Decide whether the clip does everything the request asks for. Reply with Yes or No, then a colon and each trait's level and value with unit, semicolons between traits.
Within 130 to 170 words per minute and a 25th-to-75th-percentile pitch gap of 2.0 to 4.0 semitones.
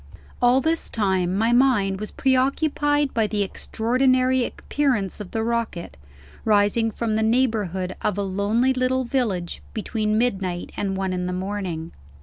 No: average, 150 wpm; average, 4.8 semitones